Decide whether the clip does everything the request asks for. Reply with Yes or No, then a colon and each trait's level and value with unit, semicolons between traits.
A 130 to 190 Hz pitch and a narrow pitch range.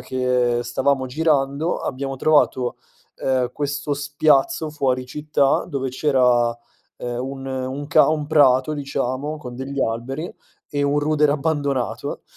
Yes: medium, 140 Hz; narrow, 2.3 semitones